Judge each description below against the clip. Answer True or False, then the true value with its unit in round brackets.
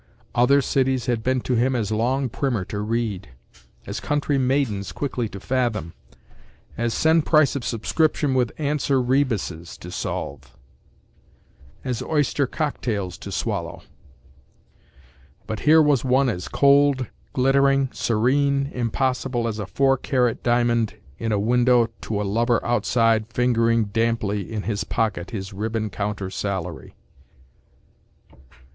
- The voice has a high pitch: False (120 Hz)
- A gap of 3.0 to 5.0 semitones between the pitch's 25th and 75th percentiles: True (3.7 semitones)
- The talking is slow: True (130 wpm)